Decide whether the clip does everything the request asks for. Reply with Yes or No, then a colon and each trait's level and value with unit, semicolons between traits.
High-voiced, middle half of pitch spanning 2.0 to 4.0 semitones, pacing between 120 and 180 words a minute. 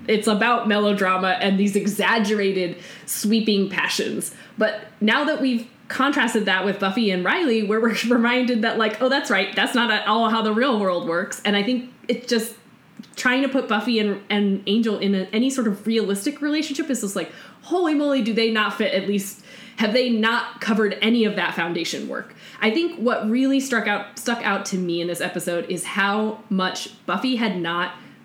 No: high, 220 Hz; average, 3.2 semitones; average, 200 wpm